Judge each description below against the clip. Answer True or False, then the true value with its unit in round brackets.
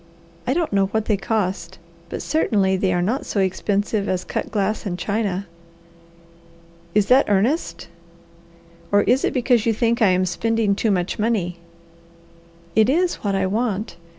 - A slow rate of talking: False (160 wpm)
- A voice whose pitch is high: True (205 Hz)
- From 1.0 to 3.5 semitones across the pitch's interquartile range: True (3.1 semitones)